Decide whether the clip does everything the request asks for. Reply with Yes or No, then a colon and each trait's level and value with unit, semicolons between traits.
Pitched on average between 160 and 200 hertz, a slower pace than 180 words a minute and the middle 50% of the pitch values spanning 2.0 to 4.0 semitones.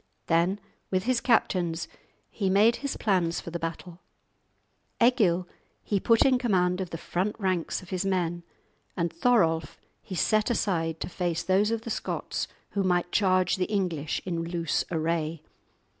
Yes: medium, 185 Hz; average, 160 wpm; average, 3.4 semitones